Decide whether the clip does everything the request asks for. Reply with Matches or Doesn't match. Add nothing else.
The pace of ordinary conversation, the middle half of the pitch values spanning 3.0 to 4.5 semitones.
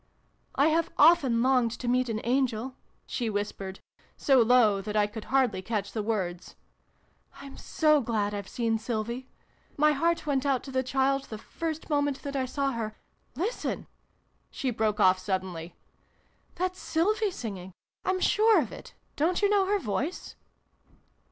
Doesn't match